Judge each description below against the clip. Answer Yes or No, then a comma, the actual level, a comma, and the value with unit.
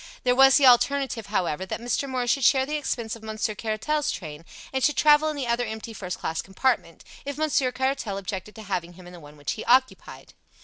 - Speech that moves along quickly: Yes, fast, 220 wpm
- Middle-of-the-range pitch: No, high, 235 Hz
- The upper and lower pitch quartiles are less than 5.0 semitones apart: No, average, 5.3 semitones